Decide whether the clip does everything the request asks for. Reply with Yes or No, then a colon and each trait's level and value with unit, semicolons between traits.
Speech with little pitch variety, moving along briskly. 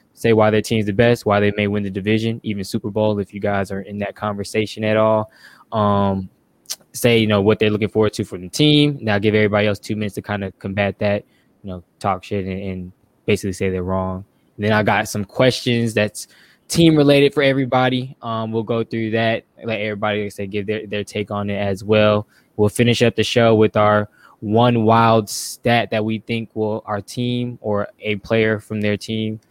Yes: narrow, 1.8 semitones; fast, 215 wpm